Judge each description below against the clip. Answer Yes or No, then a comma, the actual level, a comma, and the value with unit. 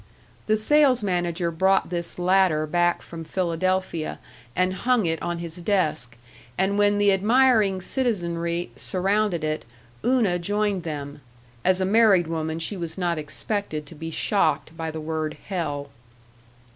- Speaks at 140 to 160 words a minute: Yes, average, 145 wpm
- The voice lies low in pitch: No, medium, 175 Hz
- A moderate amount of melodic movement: Yes, average, 3.8 semitones